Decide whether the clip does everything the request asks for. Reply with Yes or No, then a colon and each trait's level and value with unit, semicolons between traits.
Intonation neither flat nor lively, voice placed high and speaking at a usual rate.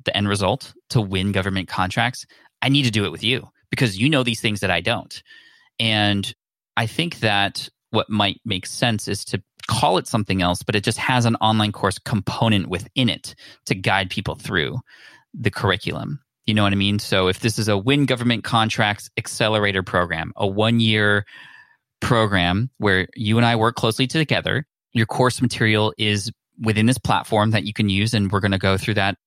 No: average, 3.3 semitones; low, 110 Hz; average, 195 wpm